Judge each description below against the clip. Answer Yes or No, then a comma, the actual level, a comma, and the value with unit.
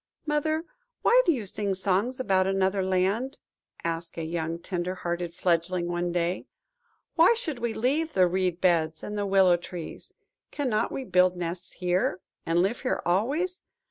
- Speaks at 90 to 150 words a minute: No, average, 165 wpm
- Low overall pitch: No, medium, 185 Hz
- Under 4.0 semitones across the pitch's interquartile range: No, wide, 5.5 semitones